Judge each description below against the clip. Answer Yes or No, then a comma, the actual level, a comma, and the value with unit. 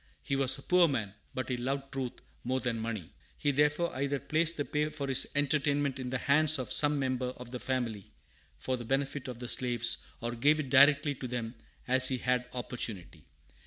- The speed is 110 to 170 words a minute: No, average, 200 wpm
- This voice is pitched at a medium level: No, low, 130 Hz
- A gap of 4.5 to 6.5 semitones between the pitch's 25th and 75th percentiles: No, narrow, 2.6 semitones